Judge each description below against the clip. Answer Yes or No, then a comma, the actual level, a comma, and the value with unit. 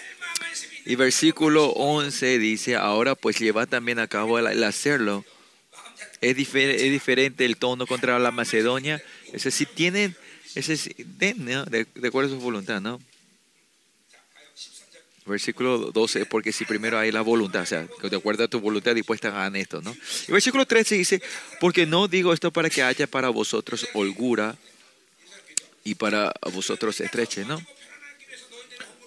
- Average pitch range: No, wide, 6.0 semitones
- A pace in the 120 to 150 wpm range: Yes, average, 145 wpm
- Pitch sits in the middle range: No, low, 125 Hz